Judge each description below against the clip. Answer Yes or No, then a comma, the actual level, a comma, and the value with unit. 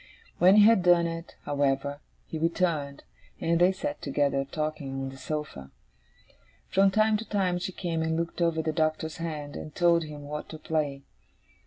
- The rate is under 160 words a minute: No, average, 175 wpm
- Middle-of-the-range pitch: Yes, medium, 160 Hz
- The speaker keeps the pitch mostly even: No, average, 3.3 semitones